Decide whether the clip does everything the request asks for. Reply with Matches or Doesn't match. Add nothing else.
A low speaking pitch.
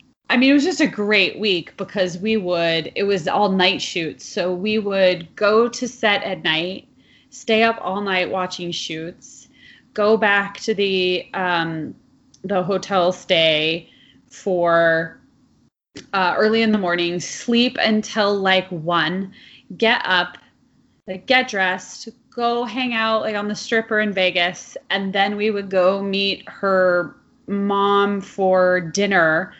Doesn't match